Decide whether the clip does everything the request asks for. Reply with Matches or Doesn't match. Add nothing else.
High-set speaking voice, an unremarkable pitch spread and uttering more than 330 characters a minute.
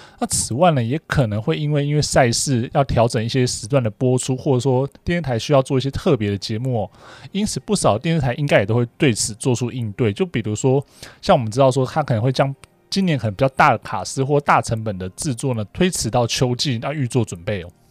Doesn't match